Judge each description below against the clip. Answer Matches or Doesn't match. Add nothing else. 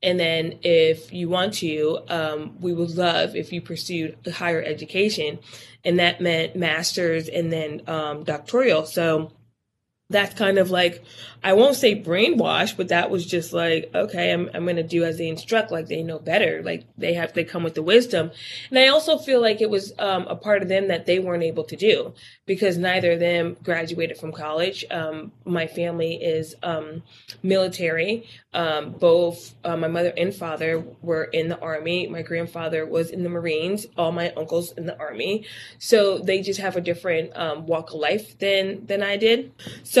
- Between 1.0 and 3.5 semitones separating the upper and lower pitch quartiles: Matches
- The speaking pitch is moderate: Matches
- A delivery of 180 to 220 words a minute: Matches